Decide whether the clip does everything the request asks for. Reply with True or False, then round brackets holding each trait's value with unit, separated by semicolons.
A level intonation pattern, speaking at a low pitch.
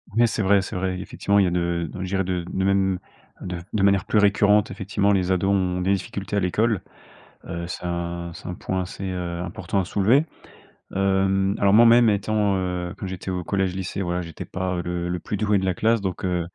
True (2.0 semitones; 95 Hz)